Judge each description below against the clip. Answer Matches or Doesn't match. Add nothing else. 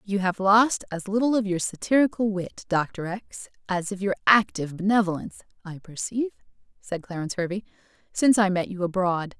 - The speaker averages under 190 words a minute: Matches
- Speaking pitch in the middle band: Doesn't match